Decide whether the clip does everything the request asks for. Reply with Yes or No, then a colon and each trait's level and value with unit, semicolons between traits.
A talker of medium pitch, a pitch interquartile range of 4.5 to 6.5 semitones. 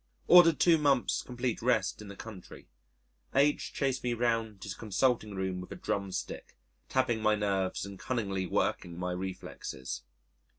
No: low, 110 Hz; average, 4.8 semitones